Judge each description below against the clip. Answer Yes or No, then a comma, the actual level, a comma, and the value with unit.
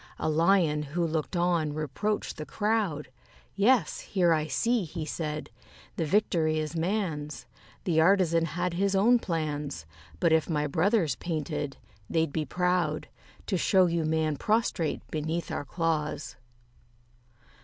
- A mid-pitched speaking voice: Yes, medium, 165 Hz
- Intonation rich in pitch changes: No, average, 3.1 semitones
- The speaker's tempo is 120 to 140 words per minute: Yes, slow, 135 wpm